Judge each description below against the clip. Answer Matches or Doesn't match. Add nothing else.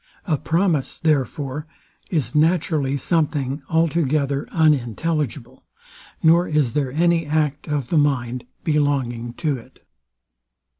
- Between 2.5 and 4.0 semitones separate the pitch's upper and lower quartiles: Matches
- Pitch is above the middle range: Doesn't match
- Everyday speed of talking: Doesn't match